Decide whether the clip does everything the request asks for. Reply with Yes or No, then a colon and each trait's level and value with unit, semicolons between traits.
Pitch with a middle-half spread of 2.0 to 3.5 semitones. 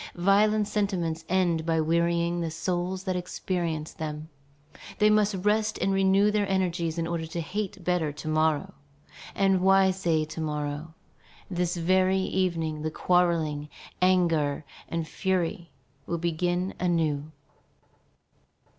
Yes: average, 2.8 semitones